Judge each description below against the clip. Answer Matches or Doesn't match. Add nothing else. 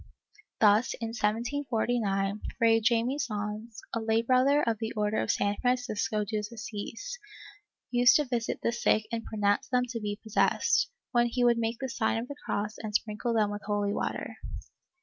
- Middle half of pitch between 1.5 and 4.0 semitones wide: Matches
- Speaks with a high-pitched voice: Matches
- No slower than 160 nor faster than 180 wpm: Matches